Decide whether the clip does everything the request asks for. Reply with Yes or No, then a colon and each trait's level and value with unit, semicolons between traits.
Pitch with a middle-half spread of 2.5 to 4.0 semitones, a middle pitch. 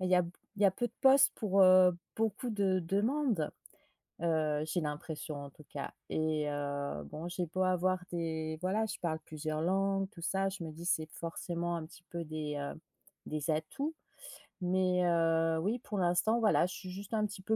Yes: average, 3.6 semitones; medium, 175 Hz